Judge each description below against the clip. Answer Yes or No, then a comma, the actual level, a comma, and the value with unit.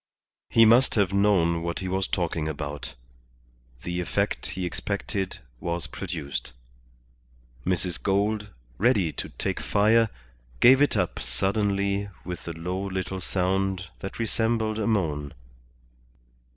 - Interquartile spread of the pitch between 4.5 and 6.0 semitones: No, average, 3.3 semitones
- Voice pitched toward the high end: No, very low, 95 Hz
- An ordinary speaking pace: No, slow, 125 wpm